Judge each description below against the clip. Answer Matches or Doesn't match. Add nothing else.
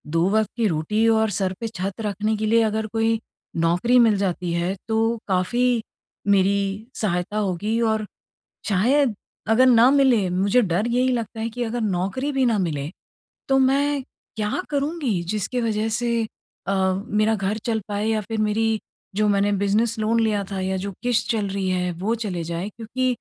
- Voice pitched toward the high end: Matches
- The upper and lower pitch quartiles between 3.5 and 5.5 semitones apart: Doesn't match